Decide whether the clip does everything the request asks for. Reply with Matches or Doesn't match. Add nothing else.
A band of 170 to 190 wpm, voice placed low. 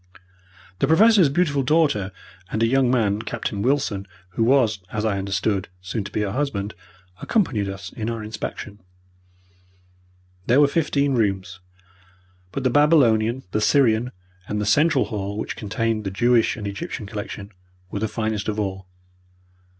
Doesn't match